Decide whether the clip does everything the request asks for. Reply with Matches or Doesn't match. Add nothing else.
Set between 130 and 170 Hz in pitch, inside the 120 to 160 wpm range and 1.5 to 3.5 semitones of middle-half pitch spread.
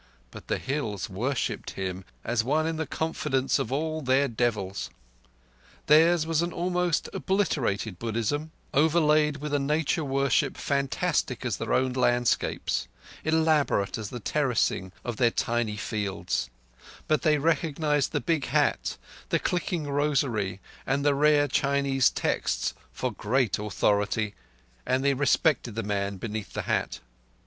Doesn't match